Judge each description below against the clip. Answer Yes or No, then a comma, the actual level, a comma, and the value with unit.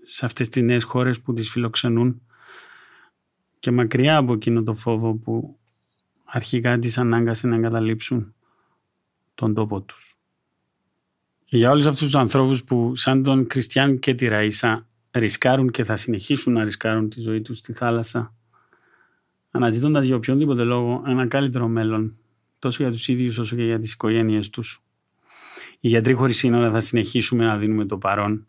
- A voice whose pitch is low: Yes, low, 120 Hz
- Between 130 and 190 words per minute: Yes, average, 155 wpm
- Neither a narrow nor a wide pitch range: No, narrow, 2.1 semitones